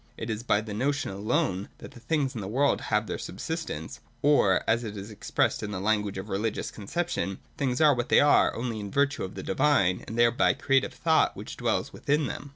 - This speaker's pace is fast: Yes, fast, 215 wpm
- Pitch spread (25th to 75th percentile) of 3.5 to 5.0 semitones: No, wide, 5.6 semitones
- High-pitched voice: No, low, 115 Hz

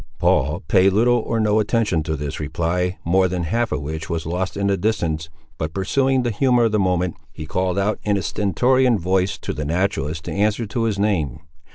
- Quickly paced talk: Yes, fast, 210 wpm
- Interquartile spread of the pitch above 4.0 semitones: Yes, average, 4.5 semitones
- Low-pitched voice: Yes, very low, 95 Hz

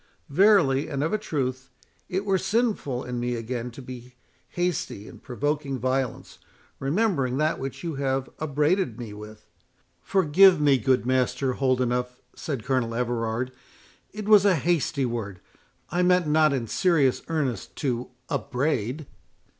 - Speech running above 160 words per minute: No, average, 140 wpm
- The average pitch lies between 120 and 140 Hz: Yes, low, 135 Hz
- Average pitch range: Yes, average, 4.3 semitones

